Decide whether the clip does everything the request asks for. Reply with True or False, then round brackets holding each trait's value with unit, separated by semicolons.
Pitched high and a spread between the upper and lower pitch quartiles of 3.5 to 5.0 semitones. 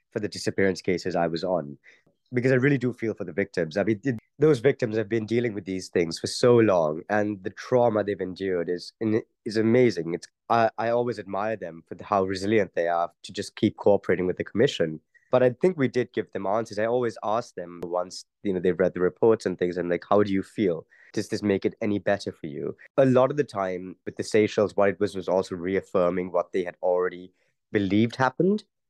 False (105 Hz; 4.2 semitones)